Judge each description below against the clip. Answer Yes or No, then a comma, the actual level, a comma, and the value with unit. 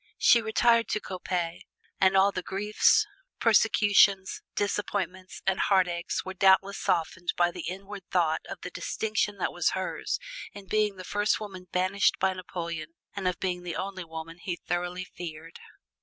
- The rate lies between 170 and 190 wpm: No, average, 155 wpm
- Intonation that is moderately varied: No, narrow, 2.3 semitones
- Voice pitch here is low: No, medium, 185 Hz